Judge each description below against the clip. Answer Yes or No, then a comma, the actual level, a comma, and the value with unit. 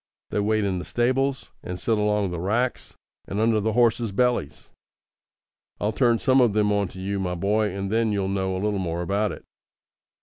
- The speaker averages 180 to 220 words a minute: Yes, average, 200 wpm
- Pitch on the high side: No, low, 105 Hz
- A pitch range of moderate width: Yes, average, 3.0 semitones